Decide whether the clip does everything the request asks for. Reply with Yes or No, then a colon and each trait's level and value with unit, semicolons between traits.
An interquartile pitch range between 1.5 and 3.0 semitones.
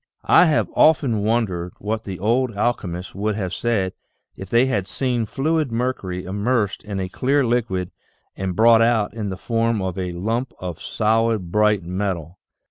No: average, 4.0 semitones